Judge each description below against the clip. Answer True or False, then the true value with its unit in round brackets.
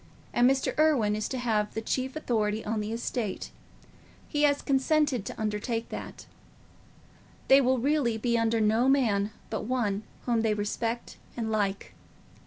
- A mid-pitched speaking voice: False (230 Hz)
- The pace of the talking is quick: False (150 wpm)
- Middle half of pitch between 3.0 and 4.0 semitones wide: True (3.5 semitones)